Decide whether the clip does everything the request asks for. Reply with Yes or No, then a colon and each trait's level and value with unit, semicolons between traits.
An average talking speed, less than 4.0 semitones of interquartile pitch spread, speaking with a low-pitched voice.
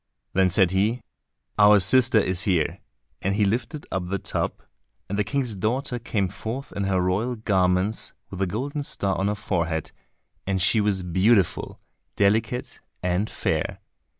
Yes: average, 155 wpm; average, 3.2 semitones; low, 100 Hz